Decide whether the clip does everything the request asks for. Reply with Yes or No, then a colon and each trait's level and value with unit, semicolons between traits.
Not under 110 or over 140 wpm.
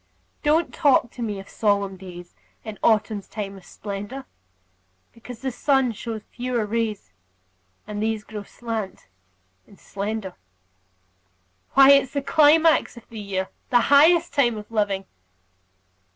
Yes: slow, 135 wpm